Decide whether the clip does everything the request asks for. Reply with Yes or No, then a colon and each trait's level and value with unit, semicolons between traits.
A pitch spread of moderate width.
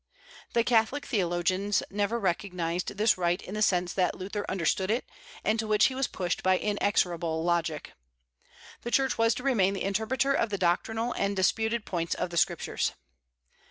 Yes: average, 3.9 semitones